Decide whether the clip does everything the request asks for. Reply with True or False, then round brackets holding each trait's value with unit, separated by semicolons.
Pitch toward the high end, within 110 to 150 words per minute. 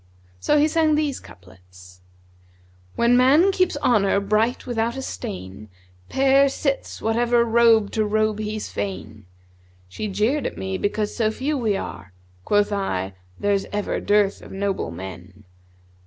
True (210 Hz; 145 wpm)